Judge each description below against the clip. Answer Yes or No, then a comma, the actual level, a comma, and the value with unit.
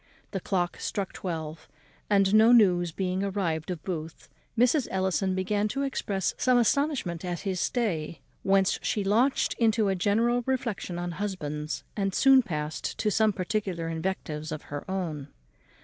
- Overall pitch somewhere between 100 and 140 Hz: No, high, 190 Hz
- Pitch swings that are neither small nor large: Yes, average, 3.9 semitones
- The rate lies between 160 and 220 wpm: No, average, 150 wpm